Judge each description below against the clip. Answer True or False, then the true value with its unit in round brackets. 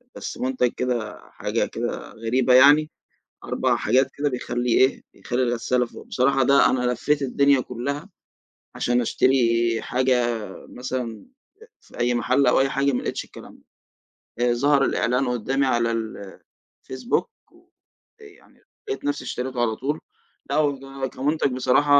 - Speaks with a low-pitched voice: True (130 Hz)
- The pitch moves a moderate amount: False (2.2 semitones)